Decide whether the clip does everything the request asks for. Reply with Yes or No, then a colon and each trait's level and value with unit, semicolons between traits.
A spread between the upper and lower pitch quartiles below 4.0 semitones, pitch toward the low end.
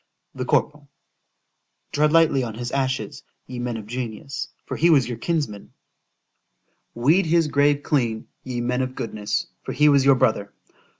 Yes: average, 3.6 semitones; low, 130 Hz